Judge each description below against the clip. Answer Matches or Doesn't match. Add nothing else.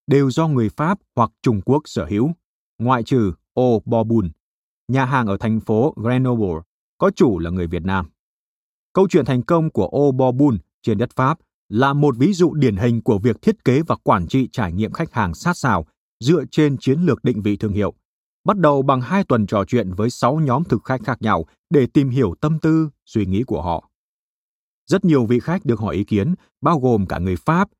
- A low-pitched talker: Matches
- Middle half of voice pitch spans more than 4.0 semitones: Matches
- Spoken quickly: Doesn't match